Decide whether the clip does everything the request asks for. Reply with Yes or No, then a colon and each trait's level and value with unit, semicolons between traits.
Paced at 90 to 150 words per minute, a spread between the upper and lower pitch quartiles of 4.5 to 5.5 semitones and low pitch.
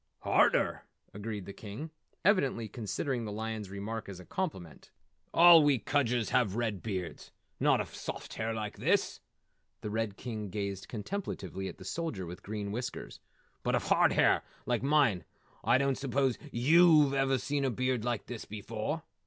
No: average, 160 wpm; average, 4.9 semitones; low, 115 Hz